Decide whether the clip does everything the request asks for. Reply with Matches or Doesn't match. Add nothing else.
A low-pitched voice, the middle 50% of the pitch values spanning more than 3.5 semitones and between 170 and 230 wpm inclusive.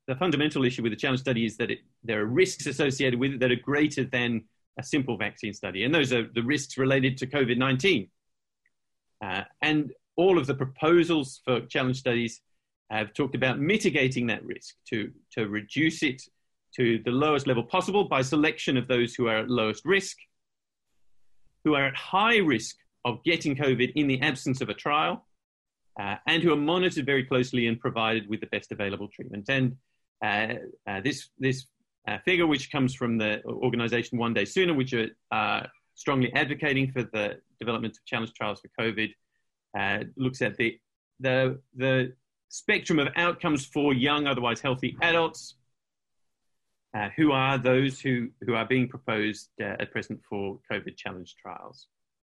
Matches